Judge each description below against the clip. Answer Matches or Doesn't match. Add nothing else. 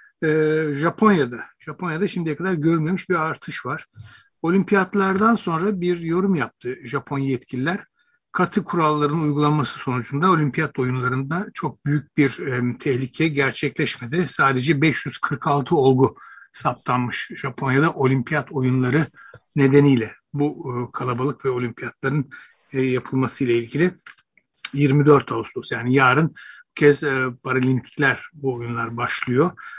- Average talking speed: Matches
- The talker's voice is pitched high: Doesn't match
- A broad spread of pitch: Doesn't match